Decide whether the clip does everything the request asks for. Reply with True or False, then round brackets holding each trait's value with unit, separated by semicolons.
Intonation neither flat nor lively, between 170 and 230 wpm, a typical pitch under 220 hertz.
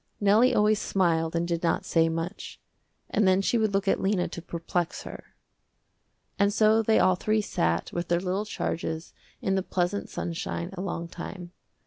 True (3.1 semitones; 175 wpm; 185 Hz)